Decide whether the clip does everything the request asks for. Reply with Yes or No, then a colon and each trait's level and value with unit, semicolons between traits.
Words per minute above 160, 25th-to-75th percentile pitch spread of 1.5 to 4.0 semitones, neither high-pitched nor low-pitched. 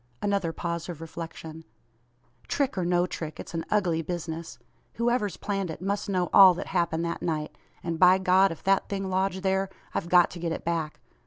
Yes: average, 190 wpm; narrow, 2.6 semitones; medium, 175 Hz